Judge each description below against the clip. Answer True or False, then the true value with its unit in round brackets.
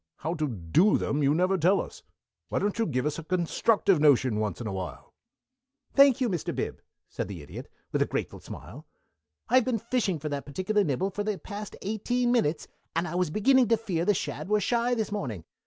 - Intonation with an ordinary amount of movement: False (6.8 semitones)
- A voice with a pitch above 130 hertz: True (185 Hz)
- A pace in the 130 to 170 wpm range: False (205 wpm)